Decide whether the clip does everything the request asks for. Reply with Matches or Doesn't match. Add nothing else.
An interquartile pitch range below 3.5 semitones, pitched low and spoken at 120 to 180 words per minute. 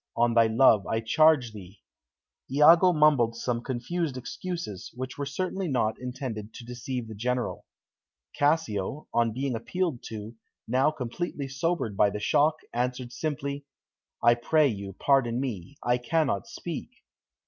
Doesn't match